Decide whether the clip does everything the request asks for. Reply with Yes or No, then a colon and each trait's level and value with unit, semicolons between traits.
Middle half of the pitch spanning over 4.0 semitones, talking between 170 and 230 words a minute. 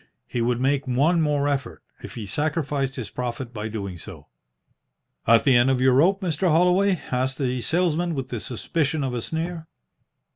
Yes: average, 4.6 semitones; average, 180 wpm